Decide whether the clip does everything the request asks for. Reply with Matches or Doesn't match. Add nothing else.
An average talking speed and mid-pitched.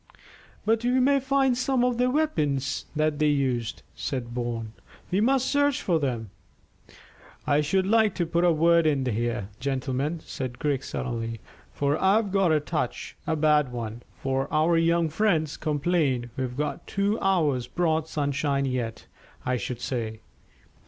Matches